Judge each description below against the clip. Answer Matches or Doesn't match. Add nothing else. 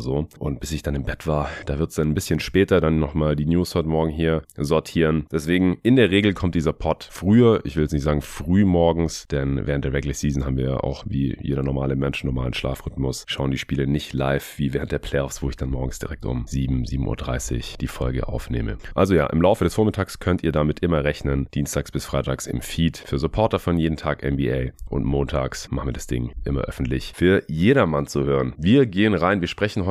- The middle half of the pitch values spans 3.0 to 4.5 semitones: Matches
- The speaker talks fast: Matches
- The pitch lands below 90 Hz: Matches